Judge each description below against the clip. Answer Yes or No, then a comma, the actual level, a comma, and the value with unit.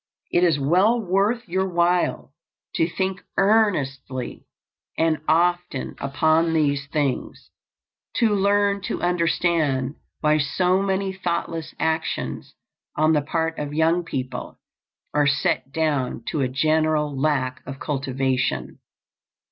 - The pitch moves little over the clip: No, average, 4.0 semitones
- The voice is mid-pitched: Yes, medium, 160 Hz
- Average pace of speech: No, slow, 115 wpm